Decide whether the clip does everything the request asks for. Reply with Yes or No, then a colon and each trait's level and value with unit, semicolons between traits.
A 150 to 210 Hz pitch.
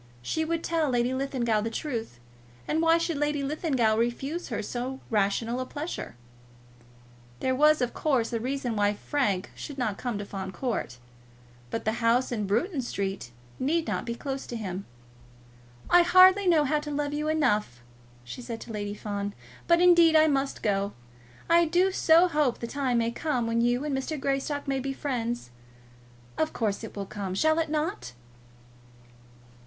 No: very high, 260 Hz